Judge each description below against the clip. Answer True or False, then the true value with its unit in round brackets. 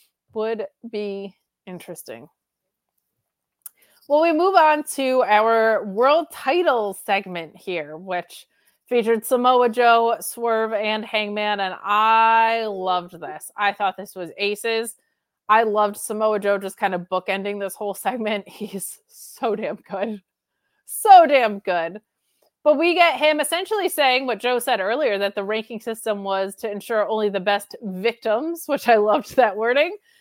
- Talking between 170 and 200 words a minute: False (145 wpm)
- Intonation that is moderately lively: True (3.8 semitones)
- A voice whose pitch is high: True (220 Hz)